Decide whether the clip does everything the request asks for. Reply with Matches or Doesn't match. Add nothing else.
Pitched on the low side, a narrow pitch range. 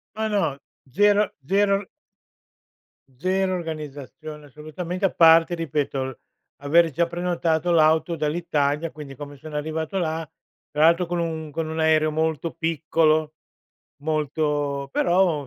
Doesn't match